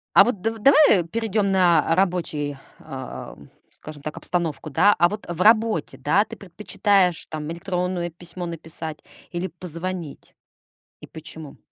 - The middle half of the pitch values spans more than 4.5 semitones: No, average, 3.5 semitones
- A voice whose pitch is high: No, medium, 175 Hz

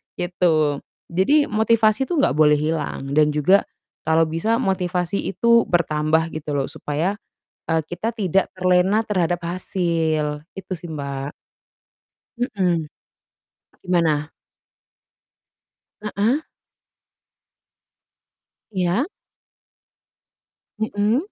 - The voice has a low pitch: No, medium, 175 Hz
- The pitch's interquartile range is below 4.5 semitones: No, average, 4.8 semitones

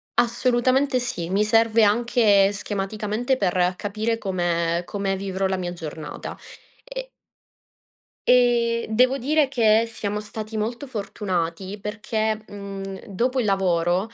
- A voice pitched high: Yes, high, 210 Hz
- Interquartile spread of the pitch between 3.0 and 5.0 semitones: Yes, average, 3.4 semitones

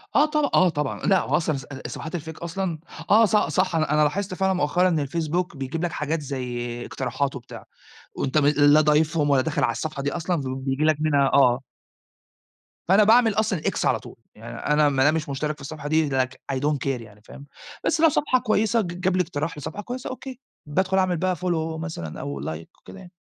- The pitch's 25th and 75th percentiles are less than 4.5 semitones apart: No, average, 5.0 semitones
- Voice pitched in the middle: Yes, medium, 155 Hz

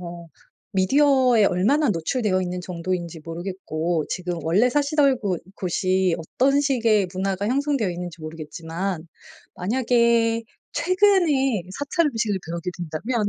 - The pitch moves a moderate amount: No, wide, 6.6 semitones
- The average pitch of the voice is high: Yes, high, 195 Hz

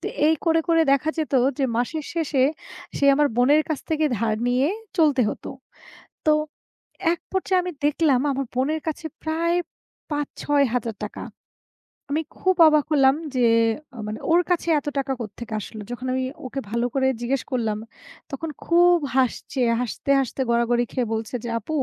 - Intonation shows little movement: No, average, 4.4 semitones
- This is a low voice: No, very high, 275 Hz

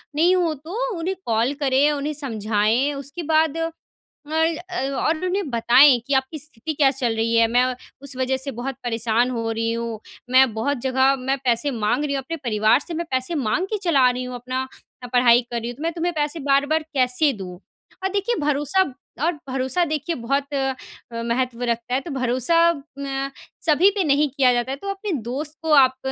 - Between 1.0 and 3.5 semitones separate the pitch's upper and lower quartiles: No, average, 3.9 semitones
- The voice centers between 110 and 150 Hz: No, very high, 270 Hz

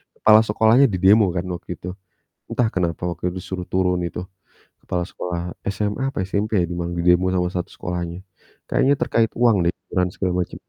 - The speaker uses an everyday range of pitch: Yes, average, 3.4 semitones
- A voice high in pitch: No, very low, 90 Hz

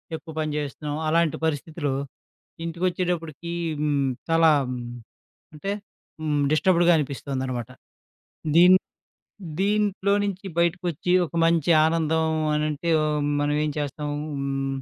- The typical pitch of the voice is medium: Yes, medium, 160 Hz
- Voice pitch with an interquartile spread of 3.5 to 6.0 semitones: No, average, 2.8 semitones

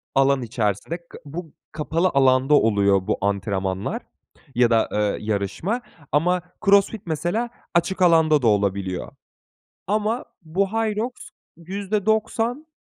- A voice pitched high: No, medium, 155 Hz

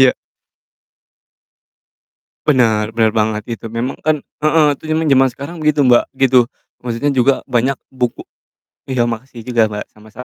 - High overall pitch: No, low, 125 Hz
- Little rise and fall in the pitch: No, average, 3.2 semitones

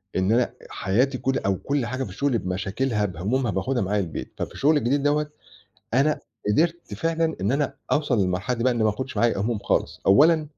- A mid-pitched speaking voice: No, low, 125 Hz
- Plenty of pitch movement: Yes, wide, 5.8 semitones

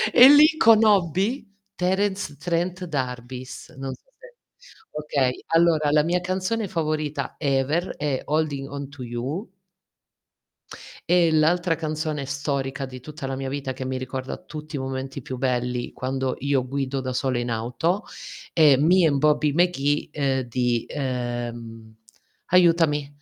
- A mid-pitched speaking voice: Yes, medium, 145 Hz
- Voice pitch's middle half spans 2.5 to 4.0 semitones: No, average, 4.4 semitones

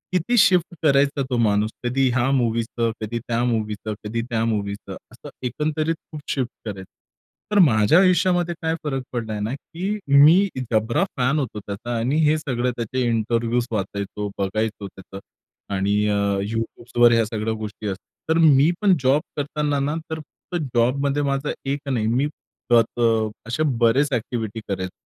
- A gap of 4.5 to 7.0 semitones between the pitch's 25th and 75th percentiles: Yes, average, 4.9 semitones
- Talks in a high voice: No, low, 120 Hz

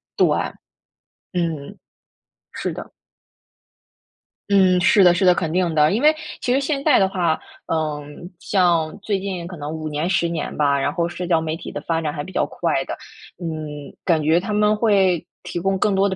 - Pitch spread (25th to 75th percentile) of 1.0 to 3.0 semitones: No, average, 3.5 semitones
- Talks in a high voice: No, medium, 175 Hz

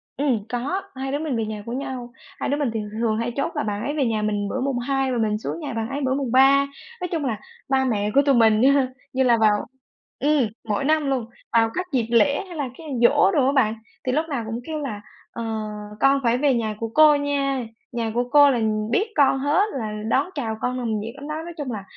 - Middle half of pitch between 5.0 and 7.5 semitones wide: No, average, 3.9 semitones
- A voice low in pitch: No, very high, 260 Hz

